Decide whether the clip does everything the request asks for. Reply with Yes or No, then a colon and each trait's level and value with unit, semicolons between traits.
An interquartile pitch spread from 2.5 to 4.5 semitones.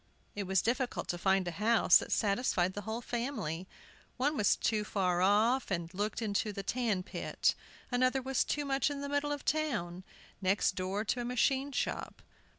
No: average, 5.3 semitones